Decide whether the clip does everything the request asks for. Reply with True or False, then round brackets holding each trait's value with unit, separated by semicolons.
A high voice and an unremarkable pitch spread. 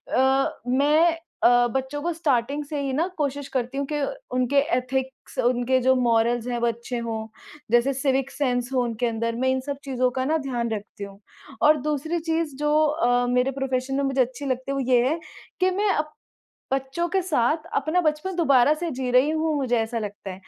True (265 Hz; 3.4 semitones)